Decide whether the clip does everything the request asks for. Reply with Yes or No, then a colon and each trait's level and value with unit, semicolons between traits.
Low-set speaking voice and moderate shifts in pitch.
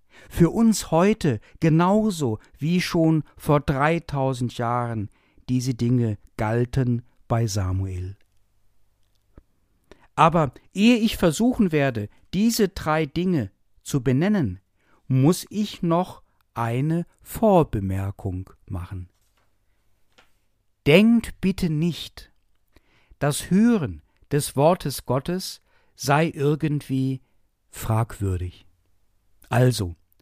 No: low, 125 Hz; wide, 8.6 semitones